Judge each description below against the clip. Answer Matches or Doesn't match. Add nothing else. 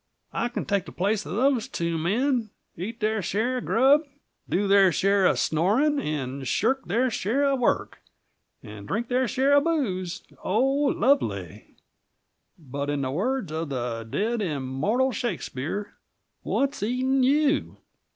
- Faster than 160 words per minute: Doesn't match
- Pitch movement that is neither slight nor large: Doesn't match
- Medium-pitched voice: Doesn't match